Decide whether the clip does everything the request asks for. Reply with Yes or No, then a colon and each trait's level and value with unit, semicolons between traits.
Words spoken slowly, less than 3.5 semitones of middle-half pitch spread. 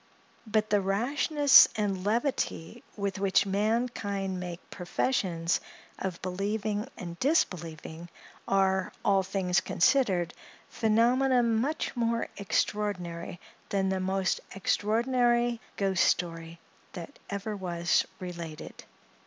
No: slow, 100 wpm; average, 4.0 semitones